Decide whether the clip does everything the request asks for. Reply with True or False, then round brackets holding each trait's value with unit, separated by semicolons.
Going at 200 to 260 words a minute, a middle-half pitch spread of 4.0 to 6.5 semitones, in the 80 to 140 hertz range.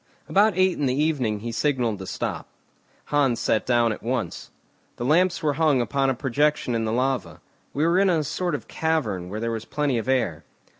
True (205 wpm; 4.8 semitones; 135 Hz)